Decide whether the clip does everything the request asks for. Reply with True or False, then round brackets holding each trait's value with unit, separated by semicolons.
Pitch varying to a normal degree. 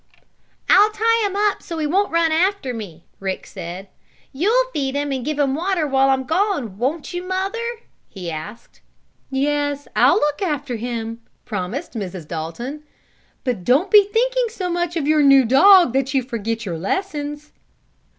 False (7.8 semitones)